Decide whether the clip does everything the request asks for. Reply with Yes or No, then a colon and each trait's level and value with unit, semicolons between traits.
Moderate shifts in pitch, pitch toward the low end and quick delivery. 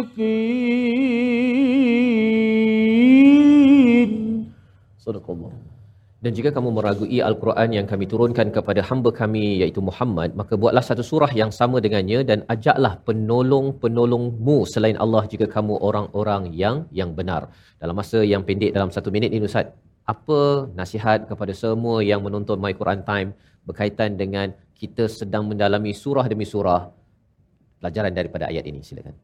Yes: average, 4.2 semitones; low, 110 Hz; fast, 130 wpm